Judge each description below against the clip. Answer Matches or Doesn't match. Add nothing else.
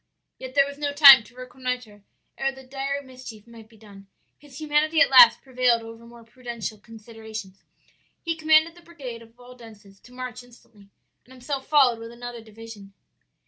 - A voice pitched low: Doesn't match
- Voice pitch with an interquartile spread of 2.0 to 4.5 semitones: Matches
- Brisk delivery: Doesn't match